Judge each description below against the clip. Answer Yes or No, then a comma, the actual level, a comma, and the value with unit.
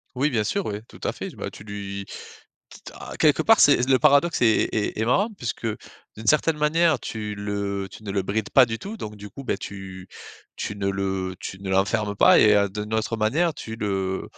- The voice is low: Yes, low, 105 Hz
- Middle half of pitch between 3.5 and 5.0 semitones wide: Yes, average, 4.0 semitones